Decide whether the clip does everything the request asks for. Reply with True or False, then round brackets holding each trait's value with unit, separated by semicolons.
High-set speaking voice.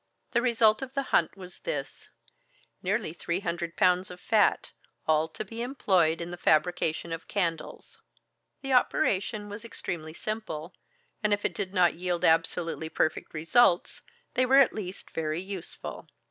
False (180 Hz)